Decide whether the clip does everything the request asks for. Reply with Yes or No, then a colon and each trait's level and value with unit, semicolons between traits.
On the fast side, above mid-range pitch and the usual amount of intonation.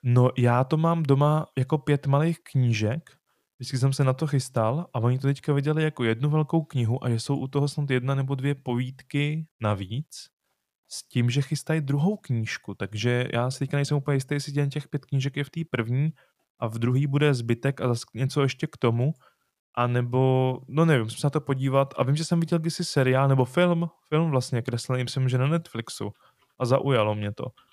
No: fast, 210 wpm; low, 135 Hz; average, 3.1 semitones